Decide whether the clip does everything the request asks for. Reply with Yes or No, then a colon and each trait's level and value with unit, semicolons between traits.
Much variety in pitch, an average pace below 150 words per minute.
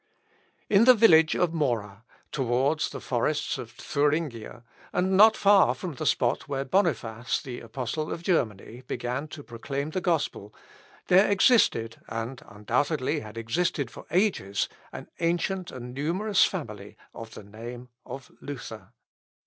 Yes: wide, 6.6 semitones; average, 140 wpm